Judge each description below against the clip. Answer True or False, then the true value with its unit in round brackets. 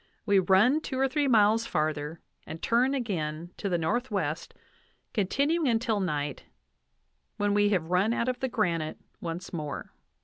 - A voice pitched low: False (205 Hz)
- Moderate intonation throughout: False (6.6 semitones)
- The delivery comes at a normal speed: True (150 wpm)